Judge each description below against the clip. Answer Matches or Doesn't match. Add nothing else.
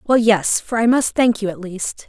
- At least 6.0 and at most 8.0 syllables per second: Doesn't match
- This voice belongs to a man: Doesn't match